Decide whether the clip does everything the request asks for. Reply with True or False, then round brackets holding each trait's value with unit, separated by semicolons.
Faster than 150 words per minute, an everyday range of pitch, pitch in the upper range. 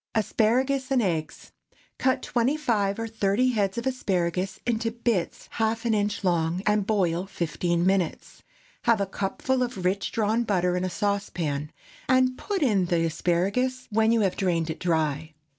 True (160 wpm; 4.8 semitones; 200 Hz)